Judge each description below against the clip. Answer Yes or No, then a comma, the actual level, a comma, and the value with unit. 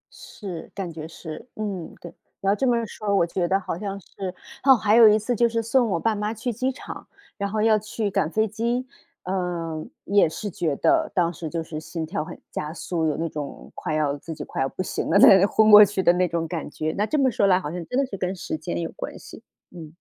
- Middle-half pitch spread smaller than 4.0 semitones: No, average, 4.7 semitones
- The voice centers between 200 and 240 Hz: No, high, 190 Hz